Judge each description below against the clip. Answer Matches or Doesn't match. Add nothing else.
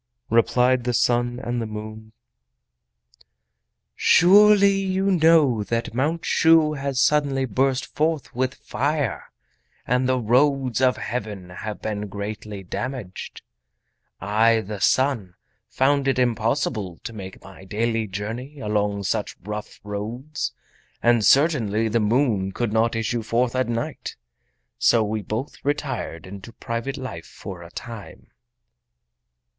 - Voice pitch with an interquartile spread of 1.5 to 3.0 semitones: Doesn't match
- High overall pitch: Doesn't match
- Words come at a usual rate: Doesn't match